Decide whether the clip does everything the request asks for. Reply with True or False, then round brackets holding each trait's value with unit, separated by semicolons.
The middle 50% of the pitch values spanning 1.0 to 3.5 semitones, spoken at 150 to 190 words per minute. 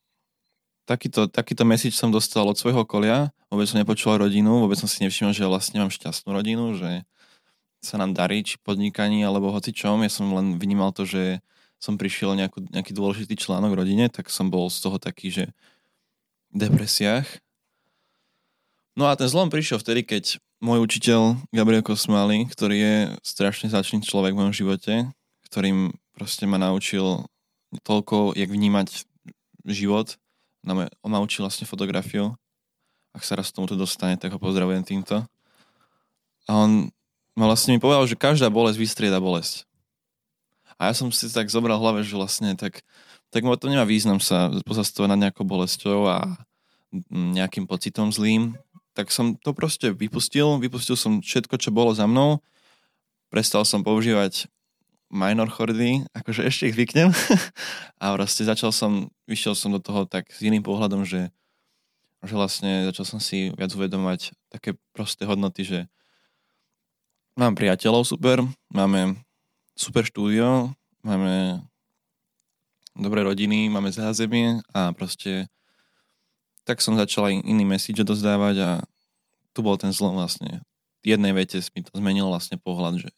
True (2.7 semitones; 155 wpm)